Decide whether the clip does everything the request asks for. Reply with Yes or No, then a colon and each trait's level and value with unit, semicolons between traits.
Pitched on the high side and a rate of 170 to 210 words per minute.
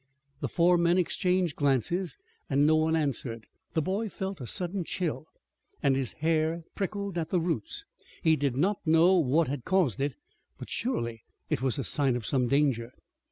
No: medium, 160 Hz; average, 175 wpm